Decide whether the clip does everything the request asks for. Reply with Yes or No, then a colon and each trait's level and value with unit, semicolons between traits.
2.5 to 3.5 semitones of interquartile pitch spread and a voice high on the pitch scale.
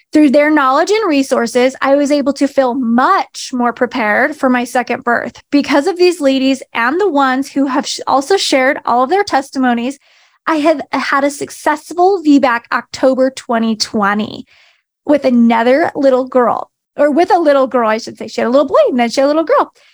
Yes: average, 2.8 semitones; very high, 270 Hz